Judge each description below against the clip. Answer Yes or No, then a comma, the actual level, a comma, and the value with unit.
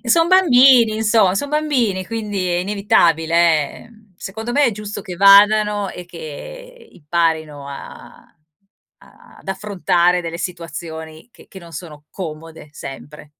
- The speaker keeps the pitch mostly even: No, average, 5.0 semitones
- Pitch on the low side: No, high, 190 Hz